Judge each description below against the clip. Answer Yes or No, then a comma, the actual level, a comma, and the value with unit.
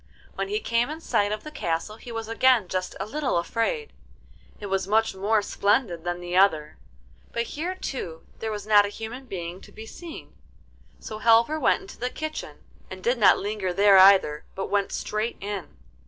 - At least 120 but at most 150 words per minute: No, average, 190 wpm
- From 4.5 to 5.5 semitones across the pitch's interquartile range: No, average, 4.0 semitones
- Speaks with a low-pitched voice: No, high, 215 Hz